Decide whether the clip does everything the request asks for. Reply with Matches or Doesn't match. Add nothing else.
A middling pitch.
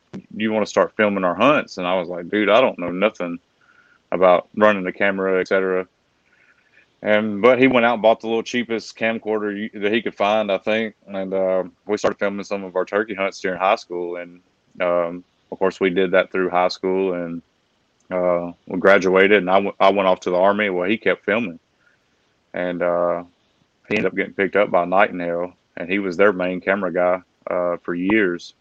Doesn't match